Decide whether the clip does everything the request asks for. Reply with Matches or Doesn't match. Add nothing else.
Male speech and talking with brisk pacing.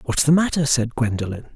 Doesn't match